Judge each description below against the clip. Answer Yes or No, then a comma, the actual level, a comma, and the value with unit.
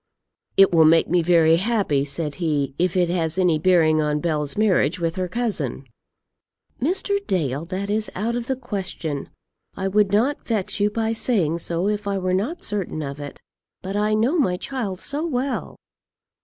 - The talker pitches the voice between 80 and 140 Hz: No, medium, 185 Hz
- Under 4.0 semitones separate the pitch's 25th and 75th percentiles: No, average, 4.9 semitones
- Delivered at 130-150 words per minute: No, average, 180 wpm